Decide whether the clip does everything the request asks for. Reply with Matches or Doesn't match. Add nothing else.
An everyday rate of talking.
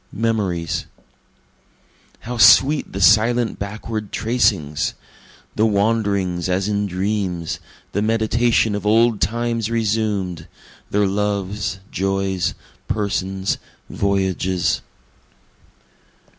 Doesn't match